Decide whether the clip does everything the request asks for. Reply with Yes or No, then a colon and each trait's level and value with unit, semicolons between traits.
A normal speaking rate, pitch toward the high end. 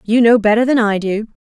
No: fast, 250 wpm; high, 220 Hz